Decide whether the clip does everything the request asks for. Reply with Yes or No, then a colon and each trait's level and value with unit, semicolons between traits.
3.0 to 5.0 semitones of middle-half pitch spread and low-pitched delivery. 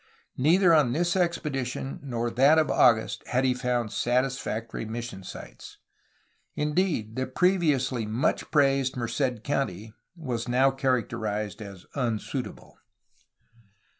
Yes: average, 3.4 semitones; low, 125 Hz